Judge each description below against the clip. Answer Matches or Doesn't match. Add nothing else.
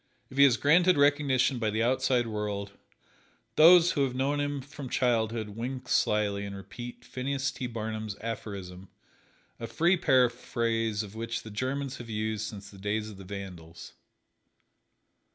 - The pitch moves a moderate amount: Matches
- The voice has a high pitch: Doesn't match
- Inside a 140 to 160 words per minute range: Matches